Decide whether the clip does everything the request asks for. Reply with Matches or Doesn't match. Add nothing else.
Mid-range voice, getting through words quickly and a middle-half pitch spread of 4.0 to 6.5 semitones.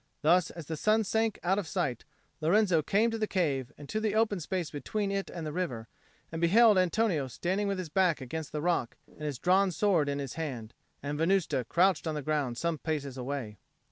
Matches